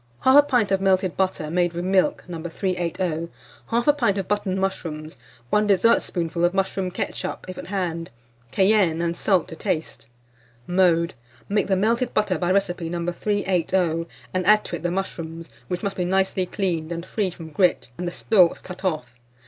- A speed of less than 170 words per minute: No, average, 175 wpm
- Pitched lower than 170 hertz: No, medium, 185 Hz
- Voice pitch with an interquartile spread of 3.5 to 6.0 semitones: No, narrow, 2.5 semitones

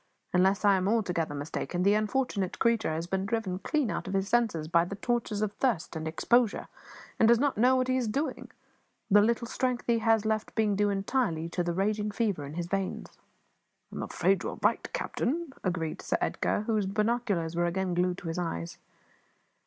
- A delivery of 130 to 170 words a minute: No, average, 200 wpm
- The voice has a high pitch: Yes, high, 205 Hz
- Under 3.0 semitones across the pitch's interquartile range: No, average, 4.6 semitones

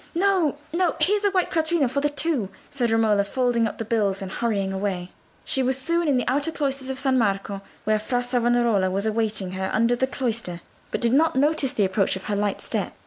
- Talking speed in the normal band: No, fast, 215 wpm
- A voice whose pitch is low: No, high, 240 Hz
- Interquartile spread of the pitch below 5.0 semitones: No, wide, 5.5 semitones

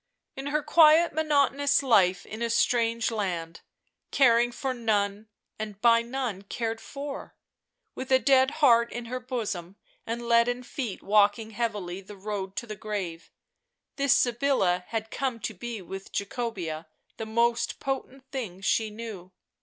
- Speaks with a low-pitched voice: No, high, 230 Hz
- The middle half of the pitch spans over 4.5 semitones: No, average, 4.2 semitones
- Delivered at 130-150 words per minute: Yes, average, 145 wpm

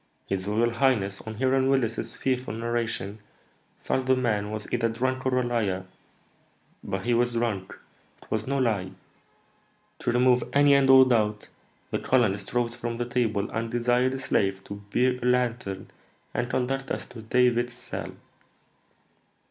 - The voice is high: No, low, 120 Hz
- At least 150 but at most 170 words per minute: Yes, average, 155 wpm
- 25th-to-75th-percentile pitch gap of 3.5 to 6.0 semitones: No, average, 2.8 semitones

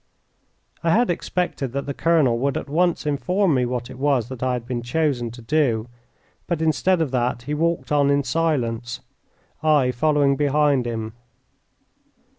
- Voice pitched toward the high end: No, medium, 140 Hz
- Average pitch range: Yes, average, 4.4 semitones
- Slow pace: No, average, 165 wpm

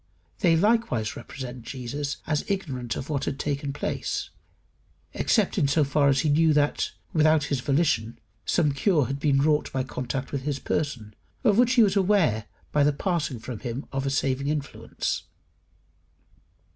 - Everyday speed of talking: Yes, average, 165 wpm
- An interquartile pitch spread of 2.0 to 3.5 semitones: Yes, average, 3.0 semitones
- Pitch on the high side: No, medium, 140 Hz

